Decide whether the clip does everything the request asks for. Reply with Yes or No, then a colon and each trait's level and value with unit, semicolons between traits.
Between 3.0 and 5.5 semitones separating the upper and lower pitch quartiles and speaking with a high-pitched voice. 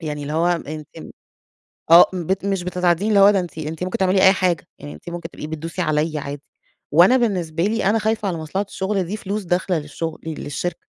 No: average, 3.5 semitones; medium, 175 Hz